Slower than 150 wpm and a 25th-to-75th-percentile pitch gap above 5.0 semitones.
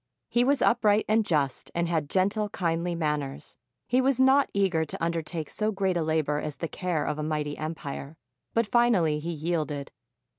No: average, 180 wpm; wide, 5.4 semitones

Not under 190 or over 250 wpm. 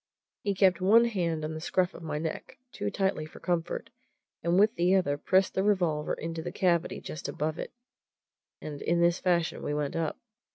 Yes: average, 195 wpm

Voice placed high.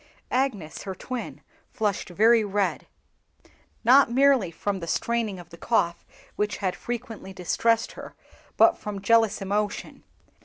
Yes: high, 210 Hz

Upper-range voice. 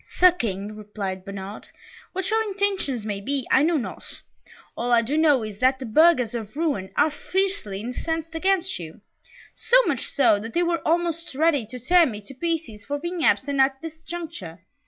Yes: very high, 280 Hz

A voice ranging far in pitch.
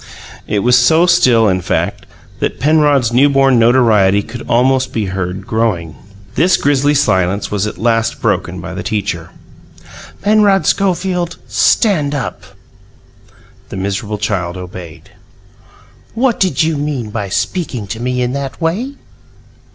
Yes: wide, 6.7 semitones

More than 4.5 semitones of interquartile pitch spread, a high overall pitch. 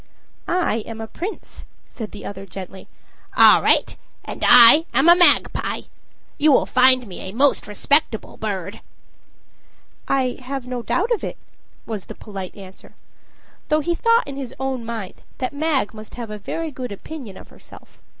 Yes: wide, 5.6 semitones; very high, 250 Hz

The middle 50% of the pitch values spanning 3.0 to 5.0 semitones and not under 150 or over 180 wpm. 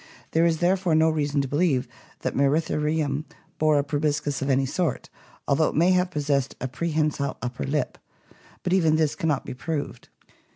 No: narrow, 2.4 semitones; average, 170 wpm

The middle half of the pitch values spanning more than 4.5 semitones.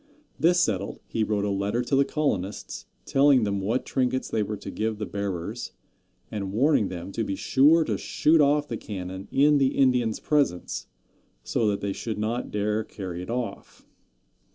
Yes: average, 5.1 semitones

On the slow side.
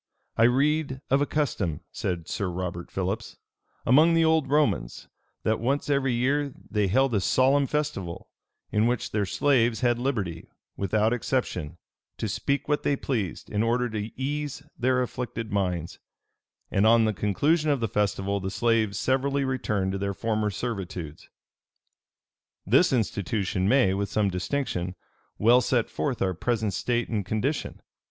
No: average, 150 wpm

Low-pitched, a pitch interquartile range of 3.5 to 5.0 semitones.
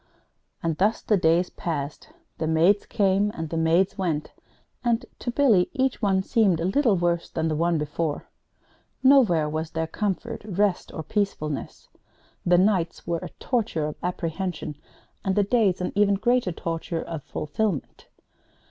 No: medium, 180 Hz; average, 4.3 semitones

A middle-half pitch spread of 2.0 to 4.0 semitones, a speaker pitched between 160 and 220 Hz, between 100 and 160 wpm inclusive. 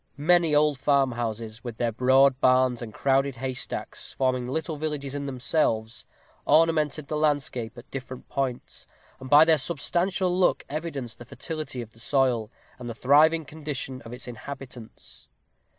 No: average, 3.6 semitones; low, 135 Hz; average, 150 wpm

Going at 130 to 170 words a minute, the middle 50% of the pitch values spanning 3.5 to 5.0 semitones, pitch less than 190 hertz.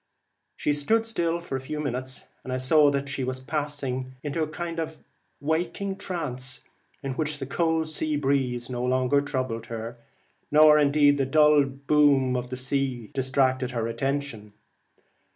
No: average, 155 wpm; average, 2.9 semitones; medium, 140 Hz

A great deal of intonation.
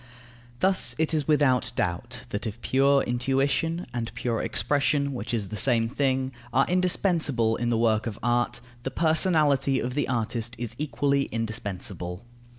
No: average, 3.7 semitones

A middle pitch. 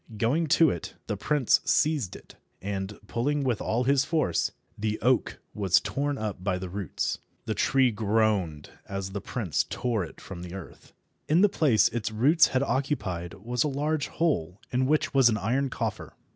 No: low, 115 Hz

